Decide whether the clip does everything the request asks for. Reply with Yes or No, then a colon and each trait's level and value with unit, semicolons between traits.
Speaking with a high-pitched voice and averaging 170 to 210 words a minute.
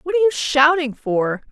Yes: very high, 295 Hz; average, 200 wpm